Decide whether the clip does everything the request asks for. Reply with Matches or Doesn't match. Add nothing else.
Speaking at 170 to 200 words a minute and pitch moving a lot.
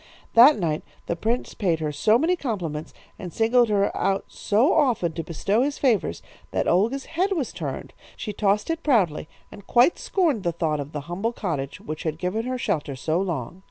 Matches